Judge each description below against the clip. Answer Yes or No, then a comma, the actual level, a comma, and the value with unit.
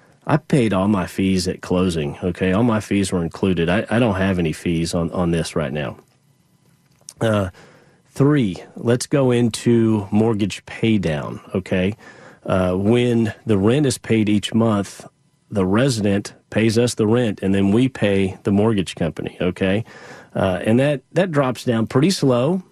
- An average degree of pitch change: Yes, average, 4.2 semitones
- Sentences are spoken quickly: No, average, 165 wpm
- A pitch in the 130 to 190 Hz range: No, low, 105 Hz